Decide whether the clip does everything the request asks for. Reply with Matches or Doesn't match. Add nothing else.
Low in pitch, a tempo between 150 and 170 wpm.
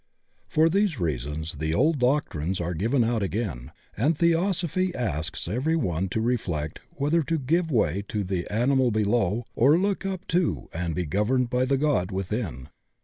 Matches